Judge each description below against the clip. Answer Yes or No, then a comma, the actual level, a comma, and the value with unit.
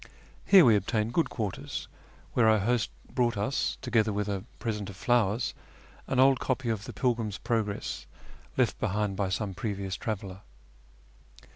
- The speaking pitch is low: Yes, low, 110 Hz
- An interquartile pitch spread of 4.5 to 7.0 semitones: No, average, 3.0 semitones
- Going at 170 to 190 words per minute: No, average, 150 wpm